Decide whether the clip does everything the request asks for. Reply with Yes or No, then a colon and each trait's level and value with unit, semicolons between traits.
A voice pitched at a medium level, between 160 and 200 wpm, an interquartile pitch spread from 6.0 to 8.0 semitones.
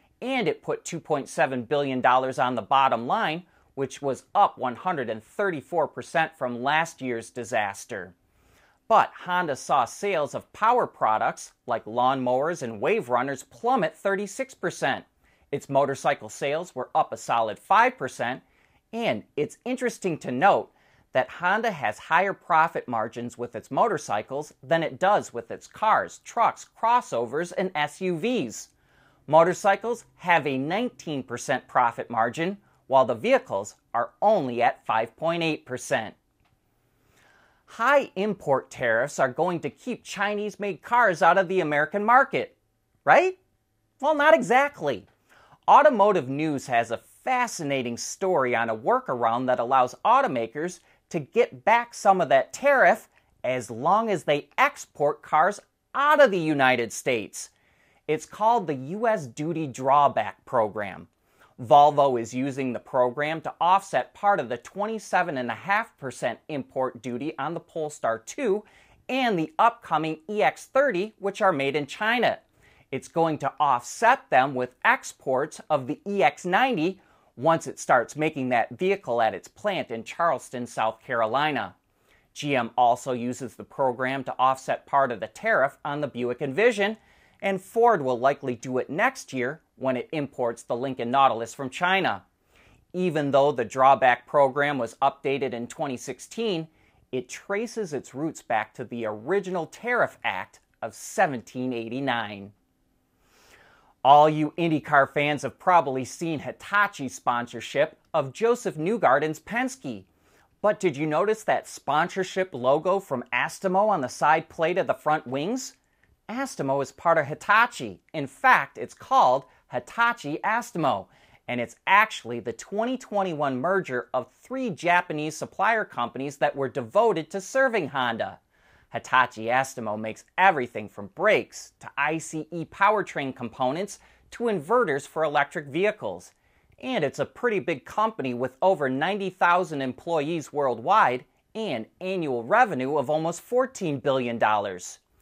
No: medium, 150 Hz; slow, 135 wpm; wide, 7.3 semitones